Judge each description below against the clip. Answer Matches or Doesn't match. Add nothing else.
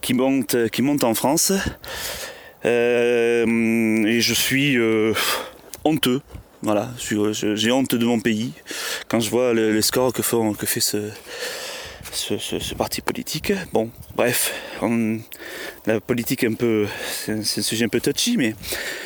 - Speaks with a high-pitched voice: Doesn't match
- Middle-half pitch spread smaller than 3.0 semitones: Matches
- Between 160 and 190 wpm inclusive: Matches